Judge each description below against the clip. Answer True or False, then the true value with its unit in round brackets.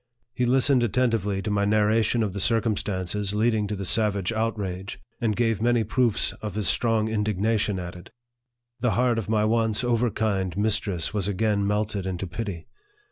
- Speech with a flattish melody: True (2.3 semitones)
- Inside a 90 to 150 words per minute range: False (170 wpm)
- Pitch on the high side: False (105 Hz)